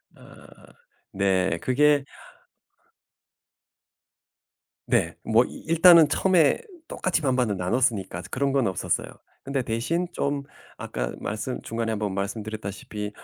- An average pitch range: No, wide, 5.7 semitones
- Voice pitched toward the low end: Yes, low, 115 Hz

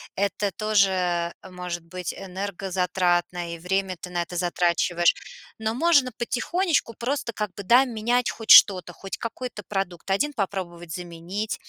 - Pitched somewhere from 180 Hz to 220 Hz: Yes, high, 190 Hz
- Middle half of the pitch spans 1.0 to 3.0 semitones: No, average, 3.8 semitones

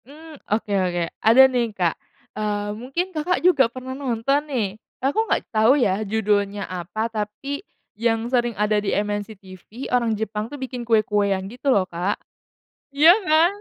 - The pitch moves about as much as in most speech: Yes, average, 4.3 semitones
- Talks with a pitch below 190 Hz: No, high, 220 Hz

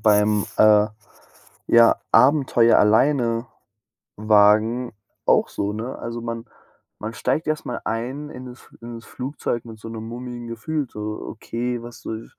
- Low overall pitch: Yes, low, 115 Hz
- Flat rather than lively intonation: Yes, narrow, 2.2 semitones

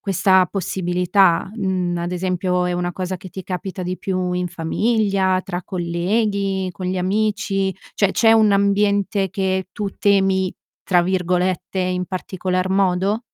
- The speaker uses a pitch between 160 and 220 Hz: Yes, medium, 185 Hz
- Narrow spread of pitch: Yes, narrow, 1.6 semitones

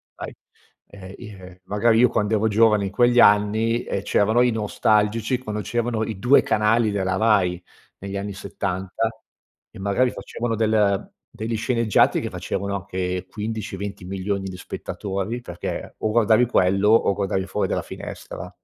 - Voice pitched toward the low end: Yes, low, 105 Hz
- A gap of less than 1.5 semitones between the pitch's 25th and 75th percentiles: No, narrow, 2.5 semitones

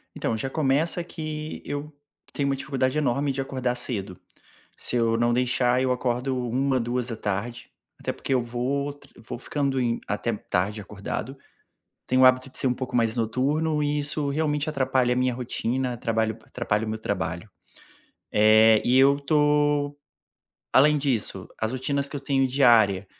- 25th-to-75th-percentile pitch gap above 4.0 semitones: No, average, 3.3 semitones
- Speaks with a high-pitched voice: No, low, 130 Hz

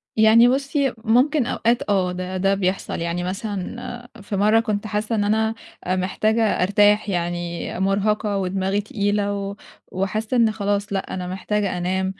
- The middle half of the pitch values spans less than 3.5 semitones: Yes, average, 2.7 semitones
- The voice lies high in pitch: Yes, high, 205 Hz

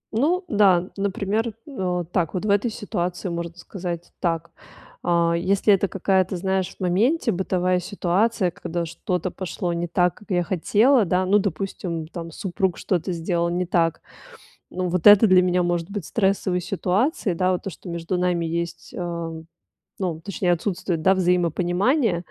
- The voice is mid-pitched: Yes, medium, 180 Hz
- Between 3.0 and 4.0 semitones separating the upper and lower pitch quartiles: No, narrow, 2.4 semitones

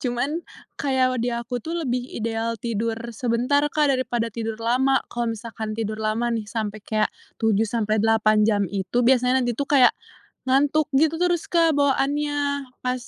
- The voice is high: Yes, high, 240 Hz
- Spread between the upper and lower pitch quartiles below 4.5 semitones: Yes, average, 3.6 semitones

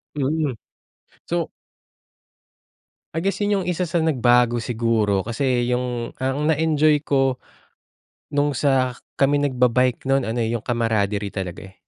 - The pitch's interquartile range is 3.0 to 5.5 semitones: Yes, average, 3.9 semitones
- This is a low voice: Yes, low, 130 Hz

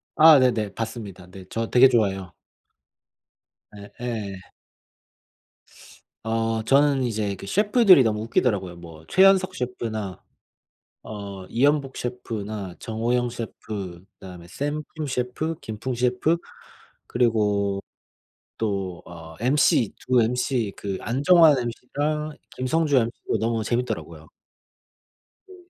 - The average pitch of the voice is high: No, low, 115 Hz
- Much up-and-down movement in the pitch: No, average, 4.9 semitones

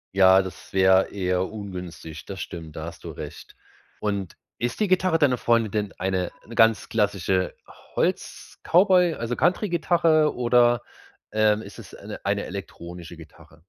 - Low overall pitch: Yes, low, 105 Hz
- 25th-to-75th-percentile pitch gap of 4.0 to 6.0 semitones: Yes, average, 5.0 semitones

